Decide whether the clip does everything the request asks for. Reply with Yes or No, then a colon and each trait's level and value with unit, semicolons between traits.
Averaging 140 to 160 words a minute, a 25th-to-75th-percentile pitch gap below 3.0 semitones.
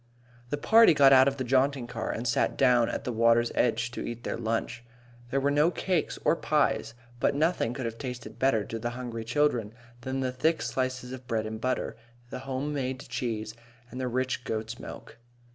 No: average, 200 wpm; narrow, 2.6 semitones